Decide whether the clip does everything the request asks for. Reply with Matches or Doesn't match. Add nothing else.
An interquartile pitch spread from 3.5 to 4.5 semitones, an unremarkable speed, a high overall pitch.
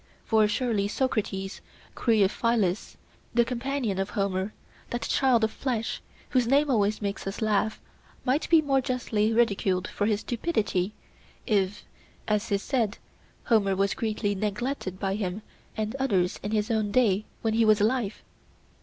Doesn't match